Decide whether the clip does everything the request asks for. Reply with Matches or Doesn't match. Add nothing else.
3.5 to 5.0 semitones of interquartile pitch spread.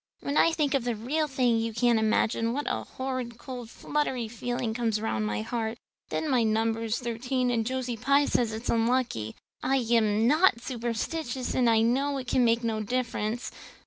Doesn't match